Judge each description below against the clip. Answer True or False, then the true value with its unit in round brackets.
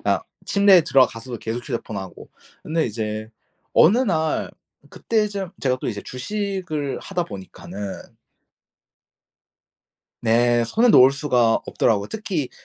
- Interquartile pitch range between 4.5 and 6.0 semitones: False (8.8 semitones)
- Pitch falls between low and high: False (130 Hz)